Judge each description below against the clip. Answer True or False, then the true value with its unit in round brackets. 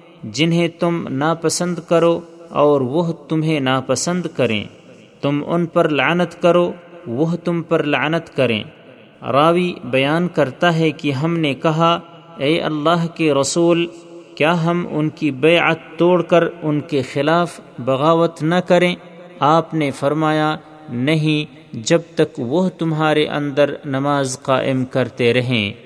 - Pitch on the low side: False (160 Hz)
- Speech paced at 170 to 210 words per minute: False (130 wpm)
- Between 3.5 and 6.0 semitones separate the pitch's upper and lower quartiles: False (3.0 semitones)